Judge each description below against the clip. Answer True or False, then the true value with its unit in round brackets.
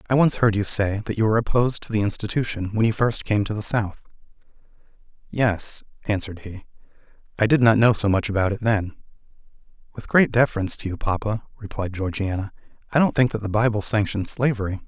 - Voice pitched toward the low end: True (105 Hz)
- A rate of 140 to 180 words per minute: False (190 wpm)